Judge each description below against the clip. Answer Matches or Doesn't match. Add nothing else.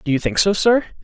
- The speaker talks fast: Matches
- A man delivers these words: Matches